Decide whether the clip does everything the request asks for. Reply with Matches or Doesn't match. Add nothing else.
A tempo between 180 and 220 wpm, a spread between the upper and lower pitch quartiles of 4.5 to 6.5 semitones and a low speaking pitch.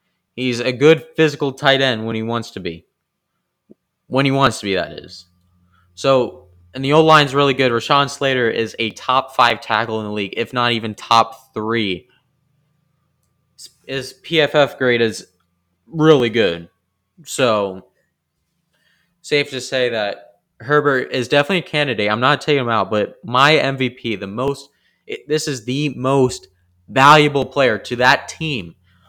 Doesn't match